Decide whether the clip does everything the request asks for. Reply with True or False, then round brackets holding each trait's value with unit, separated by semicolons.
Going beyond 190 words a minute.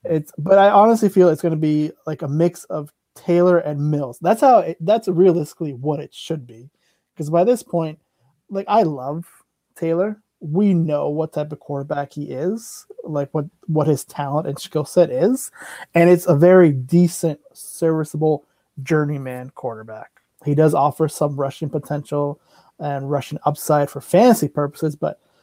False (170 wpm)